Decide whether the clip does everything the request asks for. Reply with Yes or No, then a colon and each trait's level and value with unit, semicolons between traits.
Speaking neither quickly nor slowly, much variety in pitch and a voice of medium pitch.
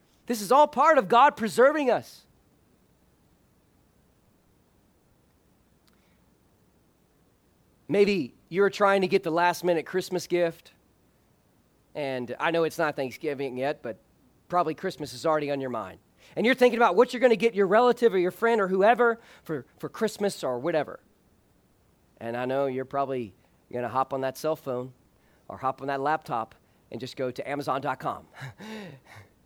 Yes: average, 155 wpm; wide, 7.4 semitones; medium, 160 Hz